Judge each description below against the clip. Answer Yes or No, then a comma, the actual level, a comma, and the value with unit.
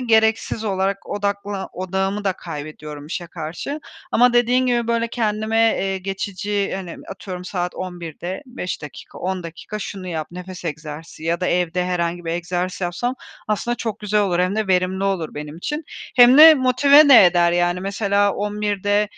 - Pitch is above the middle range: Yes, high, 195 Hz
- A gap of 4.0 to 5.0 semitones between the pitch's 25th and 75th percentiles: No, average, 3.6 semitones